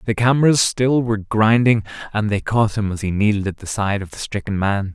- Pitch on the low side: Yes, low, 105 Hz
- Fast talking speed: Yes, fast, 230 wpm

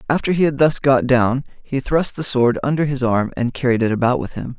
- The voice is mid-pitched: No, low, 130 Hz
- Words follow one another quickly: Yes, fast, 250 wpm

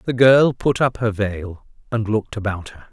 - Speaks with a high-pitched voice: No, low, 110 Hz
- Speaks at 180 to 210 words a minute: Yes, fast, 205 wpm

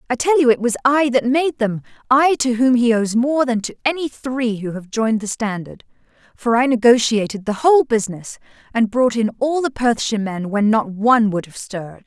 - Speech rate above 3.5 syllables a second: Yes, 5.3 syllables/s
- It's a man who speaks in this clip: No, female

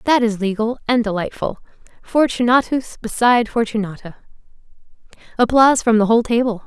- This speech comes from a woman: Yes, female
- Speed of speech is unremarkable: No, slow, 110 wpm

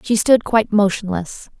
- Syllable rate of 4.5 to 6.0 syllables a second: Yes, 4.9 syllables/s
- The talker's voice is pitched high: Yes, high, 205 Hz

